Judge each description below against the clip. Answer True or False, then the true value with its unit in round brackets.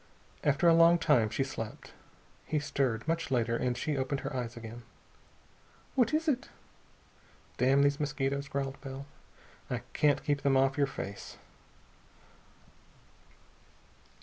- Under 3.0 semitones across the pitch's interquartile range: True (2.4 semitones)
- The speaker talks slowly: True (130 wpm)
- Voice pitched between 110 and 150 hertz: True (140 Hz)